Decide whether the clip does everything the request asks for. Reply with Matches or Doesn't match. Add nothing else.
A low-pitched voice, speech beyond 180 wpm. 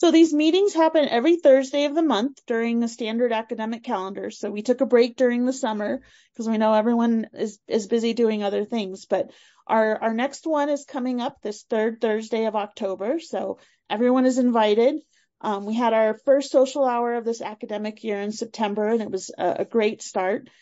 Doesn't match